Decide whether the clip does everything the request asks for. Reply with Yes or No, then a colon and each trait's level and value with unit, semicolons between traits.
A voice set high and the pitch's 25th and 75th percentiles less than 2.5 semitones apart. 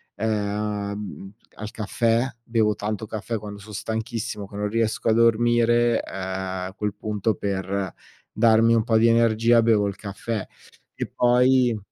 No: low, 110 Hz; narrow, 2.1 semitones